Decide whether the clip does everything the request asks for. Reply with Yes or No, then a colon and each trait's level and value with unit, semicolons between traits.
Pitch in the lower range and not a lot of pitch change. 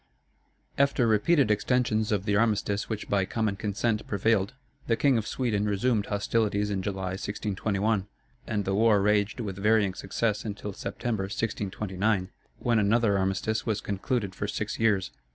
Yes: low, 105 Hz; narrow, 2.0 semitones